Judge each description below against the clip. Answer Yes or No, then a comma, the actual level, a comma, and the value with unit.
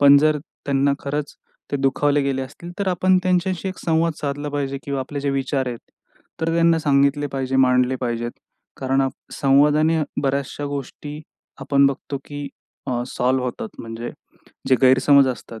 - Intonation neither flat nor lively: No, narrow, 2.1 semitones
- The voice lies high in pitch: No, medium, 140 Hz